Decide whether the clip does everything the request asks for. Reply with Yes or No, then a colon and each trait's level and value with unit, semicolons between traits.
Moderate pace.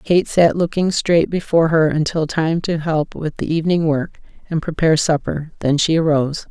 Yes: average, 185 wpm